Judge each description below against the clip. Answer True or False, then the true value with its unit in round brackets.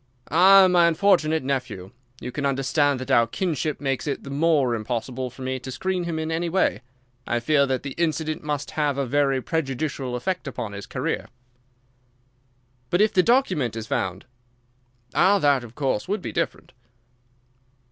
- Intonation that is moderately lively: True (4.4 semitones)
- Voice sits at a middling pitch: True (145 Hz)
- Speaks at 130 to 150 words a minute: False (165 wpm)